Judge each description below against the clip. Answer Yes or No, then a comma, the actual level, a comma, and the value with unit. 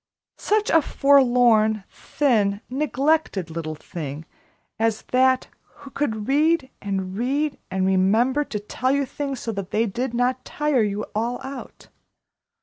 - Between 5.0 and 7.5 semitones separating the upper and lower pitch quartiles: Yes, wide, 5.4 semitones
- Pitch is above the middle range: Yes, high, 245 Hz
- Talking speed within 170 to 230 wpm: No, average, 140 wpm